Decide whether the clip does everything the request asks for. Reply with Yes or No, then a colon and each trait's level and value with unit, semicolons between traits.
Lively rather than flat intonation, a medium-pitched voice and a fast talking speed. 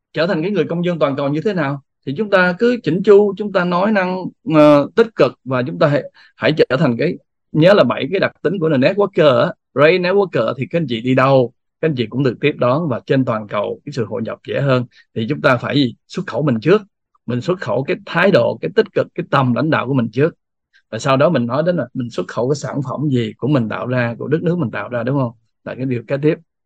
Yes: wide, 5.9 semitones; medium, 145 Hz; fast, 275 wpm